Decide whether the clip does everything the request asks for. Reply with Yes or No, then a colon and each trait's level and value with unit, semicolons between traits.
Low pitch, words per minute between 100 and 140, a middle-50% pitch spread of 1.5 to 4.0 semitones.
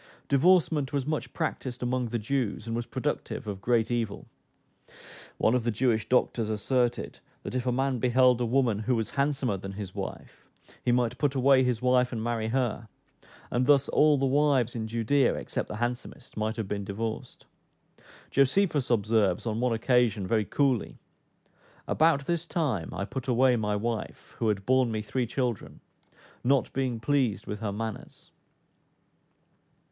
No: low, 120 Hz; average, 165 wpm; average, 3.1 semitones